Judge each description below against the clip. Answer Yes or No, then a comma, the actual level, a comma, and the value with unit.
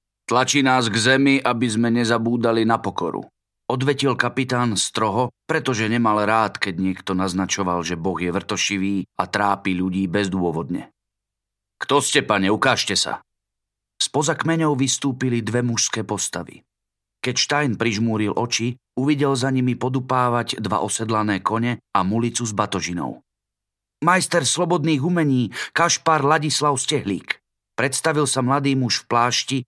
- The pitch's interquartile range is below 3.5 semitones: No, average, 4.8 semitones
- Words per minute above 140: No, average, 130 wpm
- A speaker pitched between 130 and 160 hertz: No, low, 115 Hz